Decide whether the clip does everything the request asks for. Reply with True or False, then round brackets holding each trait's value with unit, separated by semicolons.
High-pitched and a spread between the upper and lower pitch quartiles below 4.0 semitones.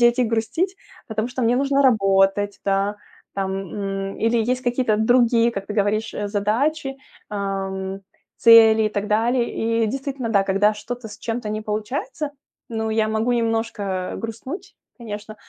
True (220 Hz; 2.7 semitones)